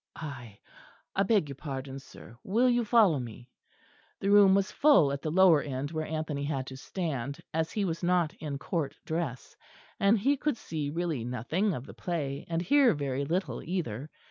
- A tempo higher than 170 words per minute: Yes, average, 185 wpm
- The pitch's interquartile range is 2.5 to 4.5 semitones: No, wide, 5.5 semitones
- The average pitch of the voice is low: No, medium, 160 Hz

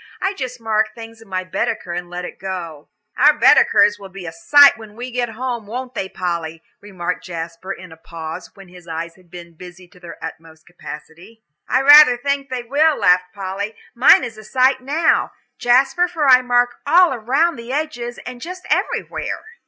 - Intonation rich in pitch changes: Yes, wide, 6.2 semitones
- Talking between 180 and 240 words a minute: Yes, average, 185 wpm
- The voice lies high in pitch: Yes, high, 220 Hz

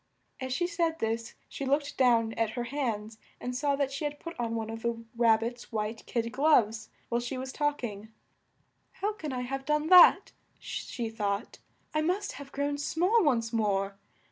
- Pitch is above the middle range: Yes, very high, 250 Hz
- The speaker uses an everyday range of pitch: Yes, average, 4.5 semitones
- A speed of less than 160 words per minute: No, average, 190 wpm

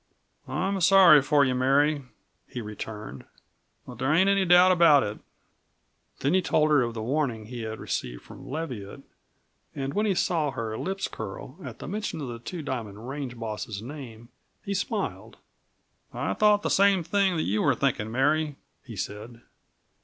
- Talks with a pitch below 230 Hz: Yes, medium, 140 Hz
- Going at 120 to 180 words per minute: Yes, average, 170 wpm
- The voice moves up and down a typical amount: No, wide, 7.0 semitones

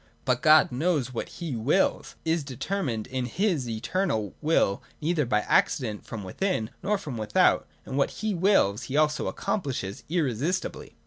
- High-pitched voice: No, medium, 140 Hz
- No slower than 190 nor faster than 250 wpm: No, average, 150 wpm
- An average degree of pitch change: No, wide, 7.0 semitones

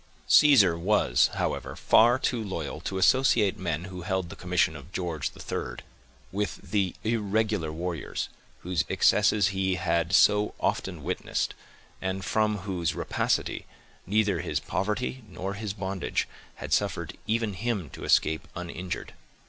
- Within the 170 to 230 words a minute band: No, slow, 135 wpm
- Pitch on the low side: Yes, very low, 95 Hz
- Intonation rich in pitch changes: No, average, 3.1 semitones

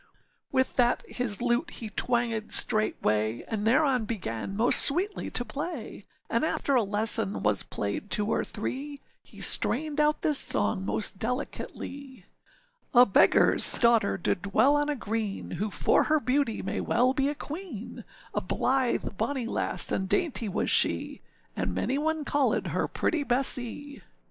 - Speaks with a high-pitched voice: Yes, high, 245 Hz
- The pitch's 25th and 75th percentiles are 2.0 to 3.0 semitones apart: No, average, 5.3 semitones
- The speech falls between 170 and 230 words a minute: No, average, 155 wpm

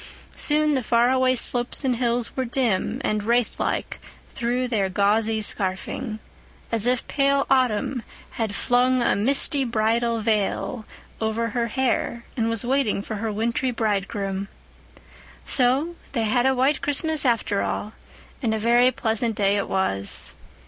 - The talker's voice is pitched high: Yes, high, 235 Hz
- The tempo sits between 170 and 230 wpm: No, average, 150 wpm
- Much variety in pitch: No, average, 3.0 semitones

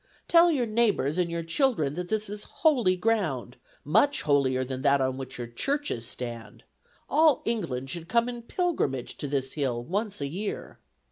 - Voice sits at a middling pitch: Yes, medium, 170 Hz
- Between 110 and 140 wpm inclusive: No, average, 175 wpm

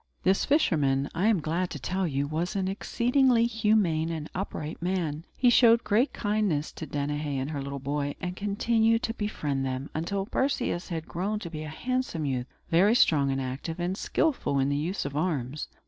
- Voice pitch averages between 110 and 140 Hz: No, medium, 170 Hz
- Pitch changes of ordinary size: No, wide, 6.3 semitones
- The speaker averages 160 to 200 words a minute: Yes, average, 190 wpm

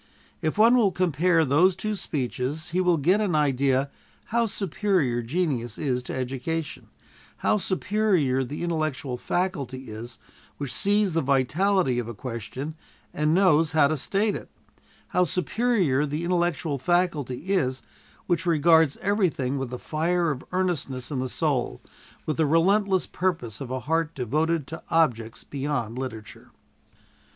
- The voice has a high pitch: No, medium, 155 Hz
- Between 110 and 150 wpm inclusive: Yes, average, 145 wpm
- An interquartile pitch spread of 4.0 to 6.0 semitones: Yes, wide, 5.6 semitones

